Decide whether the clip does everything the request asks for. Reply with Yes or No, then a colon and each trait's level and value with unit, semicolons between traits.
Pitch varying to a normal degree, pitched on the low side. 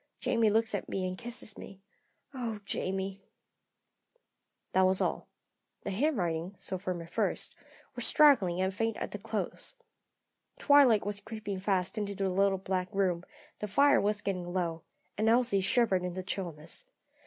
No: average, 3.0 semitones; high, 195 Hz